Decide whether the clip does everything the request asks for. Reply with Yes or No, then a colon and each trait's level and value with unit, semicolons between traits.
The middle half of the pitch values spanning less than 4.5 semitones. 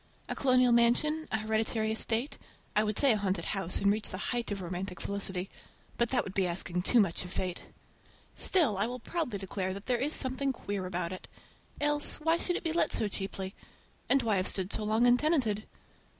No: average, 4.8 semitones